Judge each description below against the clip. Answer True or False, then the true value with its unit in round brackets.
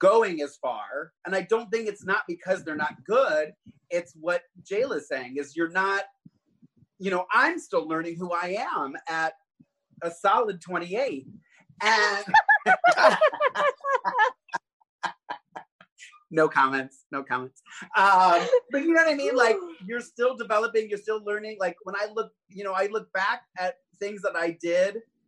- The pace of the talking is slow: False (155 wpm)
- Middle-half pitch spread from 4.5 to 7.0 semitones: True (5.5 semitones)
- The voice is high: True (195 Hz)